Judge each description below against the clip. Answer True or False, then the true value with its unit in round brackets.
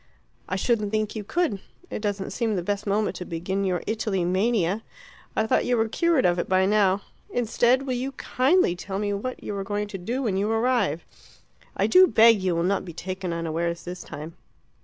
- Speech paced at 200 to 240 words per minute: True (205 wpm)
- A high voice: True (205 Hz)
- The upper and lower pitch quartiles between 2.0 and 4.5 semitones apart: True (3.7 semitones)